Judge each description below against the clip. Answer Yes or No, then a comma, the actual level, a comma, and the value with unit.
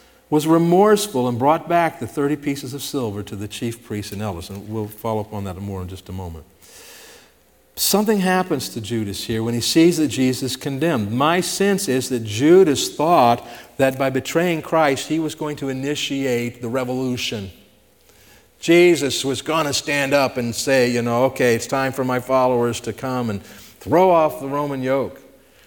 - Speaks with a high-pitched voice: No, low, 130 Hz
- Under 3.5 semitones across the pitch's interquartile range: No, average, 4.6 semitones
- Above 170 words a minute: Yes, average, 185 wpm